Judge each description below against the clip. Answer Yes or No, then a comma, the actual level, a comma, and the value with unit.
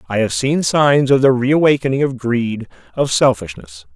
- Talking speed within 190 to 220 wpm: No, average, 165 wpm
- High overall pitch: No, low, 125 Hz